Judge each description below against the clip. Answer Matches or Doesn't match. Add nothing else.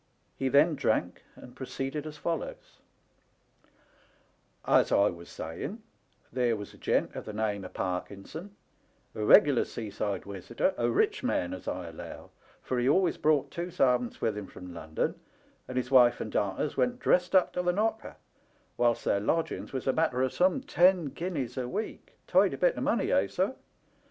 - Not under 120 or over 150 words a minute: Doesn't match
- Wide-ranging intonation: Matches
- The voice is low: Matches